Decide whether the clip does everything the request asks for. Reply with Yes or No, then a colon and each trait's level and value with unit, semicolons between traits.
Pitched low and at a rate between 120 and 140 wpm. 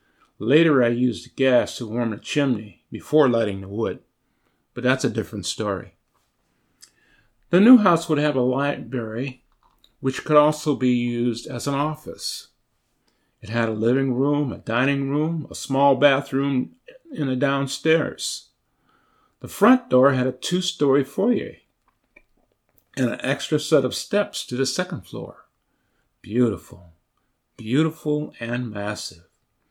Yes: low, 130 Hz; slow, 135 wpm